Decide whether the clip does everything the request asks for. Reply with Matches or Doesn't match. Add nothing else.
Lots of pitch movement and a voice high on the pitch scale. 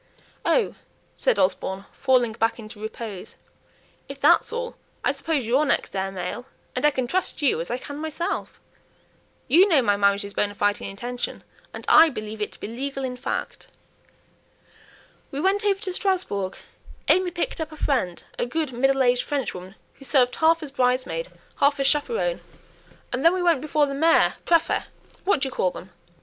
Matches